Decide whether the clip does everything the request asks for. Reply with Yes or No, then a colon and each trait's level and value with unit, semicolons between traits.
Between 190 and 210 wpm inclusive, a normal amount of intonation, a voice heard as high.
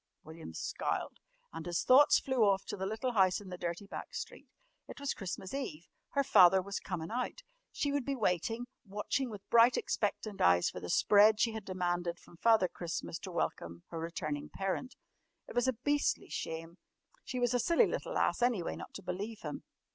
No: average, 195 wpm; wide, 5.8 semitones; high, 200 Hz